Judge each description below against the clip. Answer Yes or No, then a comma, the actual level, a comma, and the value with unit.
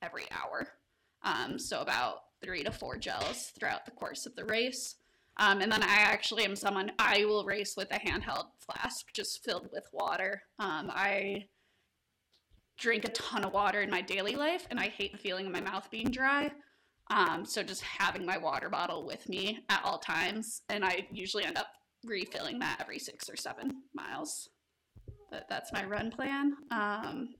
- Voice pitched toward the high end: Yes, high, 210 Hz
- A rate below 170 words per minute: No, average, 185 wpm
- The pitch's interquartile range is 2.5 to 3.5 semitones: No, average, 4.6 semitones